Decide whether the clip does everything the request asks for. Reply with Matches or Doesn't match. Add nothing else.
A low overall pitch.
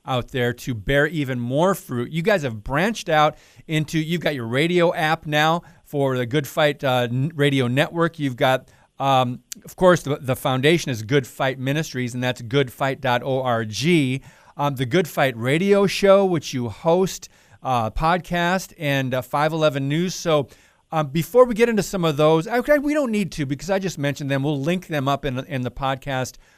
Doesn't match